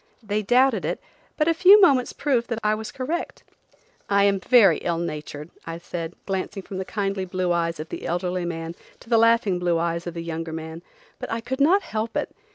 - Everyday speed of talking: No, fast, 210 wpm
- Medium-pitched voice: No, high, 195 Hz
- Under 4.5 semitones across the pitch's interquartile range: No, wide, 5.5 semitones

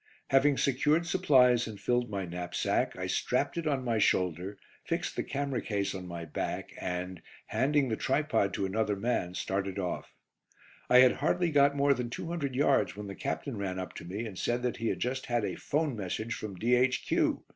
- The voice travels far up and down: Yes, wide, 5.7 semitones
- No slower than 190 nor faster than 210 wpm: Yes, average, 195 wpm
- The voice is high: No, low, 120 Hz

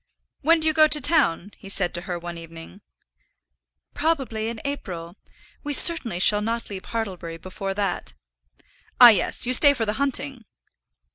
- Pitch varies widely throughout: Yes, wide, 7.7 semitones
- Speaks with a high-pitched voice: Yes, high, 220 Hz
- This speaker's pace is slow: No, average, 160 wpm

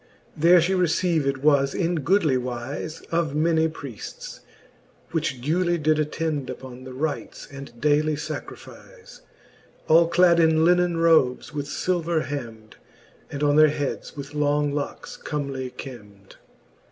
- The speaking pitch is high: No, medium, 150 Hz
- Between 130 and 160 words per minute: Yes, average, 140 wpm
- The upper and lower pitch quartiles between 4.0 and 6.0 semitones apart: No, average, 3.2 semitones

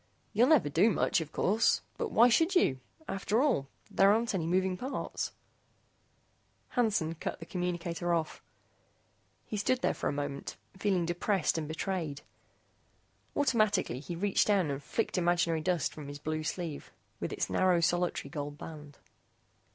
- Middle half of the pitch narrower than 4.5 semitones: No, average, 4.8 semitones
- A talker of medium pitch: Yes, medium, 175 Hz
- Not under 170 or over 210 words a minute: No, average, 150 wpm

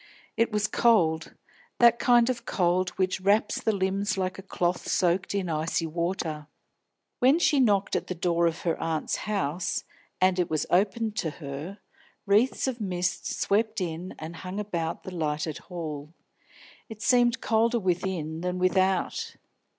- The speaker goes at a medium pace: Yes, average, 155 wpm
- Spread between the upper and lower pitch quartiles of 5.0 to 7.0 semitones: No, average, 3.9 semitones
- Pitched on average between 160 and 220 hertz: Yes, medium, 185 Hz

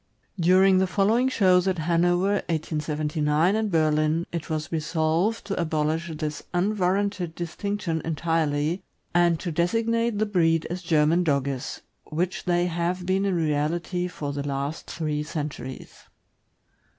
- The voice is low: No, medium, 170 Hz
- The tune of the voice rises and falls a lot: No, average, 3.3 semitones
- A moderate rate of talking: No, slow, 130 wpm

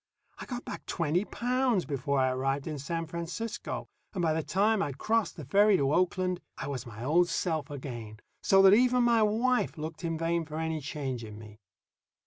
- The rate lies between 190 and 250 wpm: Yes, average, 195 wpm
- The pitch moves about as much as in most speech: No, wide, 6.2 semitones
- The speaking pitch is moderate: Yes, medium, 165 Hz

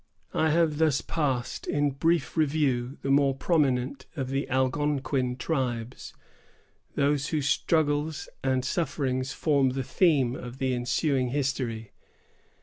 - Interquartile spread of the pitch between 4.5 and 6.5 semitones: No, narrow, 2.5 semitones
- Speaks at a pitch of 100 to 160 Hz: Yes, low, 135 Hz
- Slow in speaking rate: Yes, slow, 125 wpm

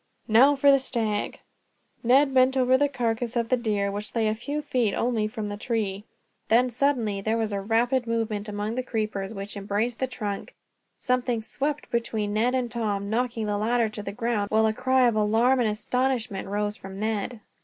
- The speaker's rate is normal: Yes, average, 195 wpm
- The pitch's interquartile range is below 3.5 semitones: Yes, average, 3.1 semitones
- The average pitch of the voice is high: Yes, high, 225 Hz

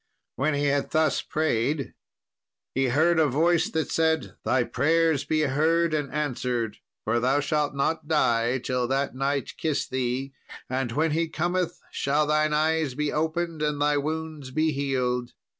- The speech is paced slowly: No, average, 160 wpm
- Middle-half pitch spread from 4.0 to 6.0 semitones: No, average, 3.2 semitones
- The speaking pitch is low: No, medium, 145 Hz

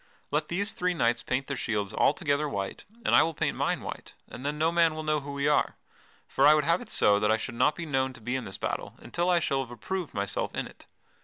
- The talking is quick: Yes, fast, 260 wpm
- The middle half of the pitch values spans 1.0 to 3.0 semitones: No, average, 4.8 semitones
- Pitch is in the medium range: Yes, medium, 145 Hz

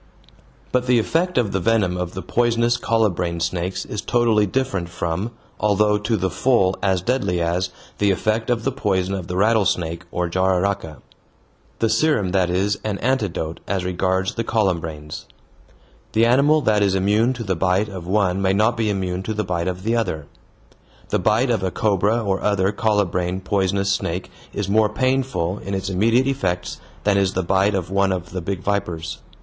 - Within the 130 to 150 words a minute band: No, average, 180 wpm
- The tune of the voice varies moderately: Yes, average, 3.3 semitones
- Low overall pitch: Yes, low, 100 Hz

